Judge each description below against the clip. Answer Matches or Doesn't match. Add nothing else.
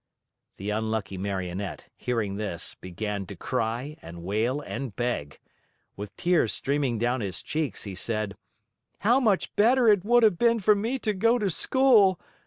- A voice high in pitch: Doesn't match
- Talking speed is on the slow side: Doesn't match